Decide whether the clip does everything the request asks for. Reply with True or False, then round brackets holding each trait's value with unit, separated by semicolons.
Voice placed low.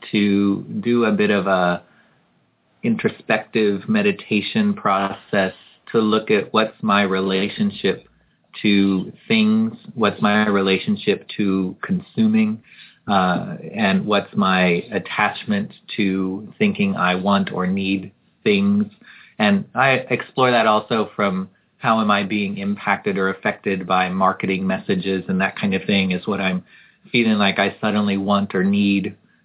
True (105 Hz)